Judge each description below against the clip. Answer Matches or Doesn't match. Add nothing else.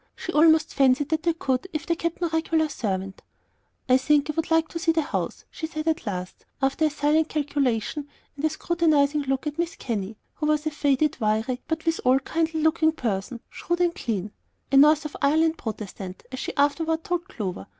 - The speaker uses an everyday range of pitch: Matches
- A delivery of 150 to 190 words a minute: Doesn't match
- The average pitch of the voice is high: Matches